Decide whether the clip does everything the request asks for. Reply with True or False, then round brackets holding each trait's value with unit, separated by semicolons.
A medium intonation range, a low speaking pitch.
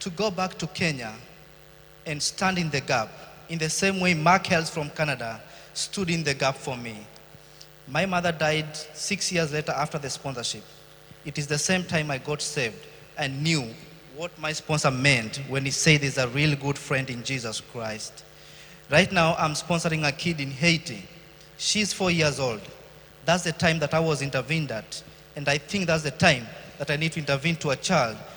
False (3.0 semitones; 150 Hz)